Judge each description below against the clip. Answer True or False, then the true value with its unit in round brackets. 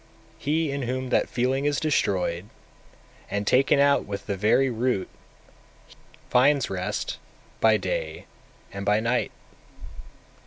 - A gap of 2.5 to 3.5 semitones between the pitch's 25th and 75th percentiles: False (5.3 semitones)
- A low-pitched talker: True (125 Hz)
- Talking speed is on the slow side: True (125 wpm)